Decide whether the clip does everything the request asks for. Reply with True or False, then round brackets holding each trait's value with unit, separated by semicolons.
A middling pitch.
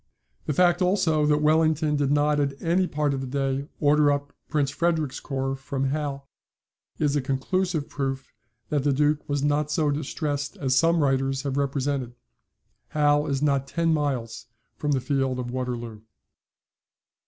True (145 Hz)